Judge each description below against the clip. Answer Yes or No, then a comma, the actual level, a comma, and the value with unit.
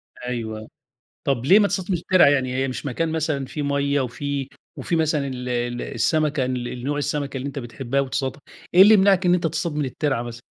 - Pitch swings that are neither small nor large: Yes, average, 3.9 semitones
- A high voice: No, medium, 140 Hz